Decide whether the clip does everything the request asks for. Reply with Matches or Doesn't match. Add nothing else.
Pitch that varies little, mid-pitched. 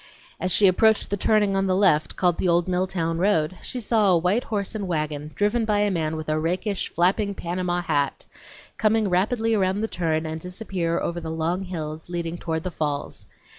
Doesn't match